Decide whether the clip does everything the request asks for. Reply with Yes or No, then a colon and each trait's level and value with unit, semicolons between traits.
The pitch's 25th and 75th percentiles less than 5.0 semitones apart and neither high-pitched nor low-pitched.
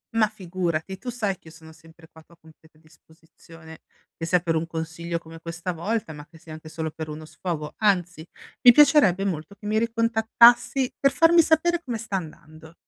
No: average, 5.3 semitones; medium, 170 Hz